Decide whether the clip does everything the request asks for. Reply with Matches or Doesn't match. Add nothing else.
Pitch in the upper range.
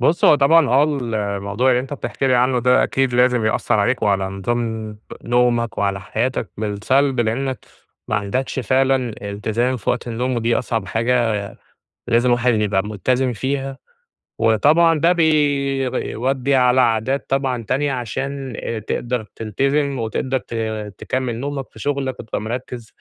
Doesn't match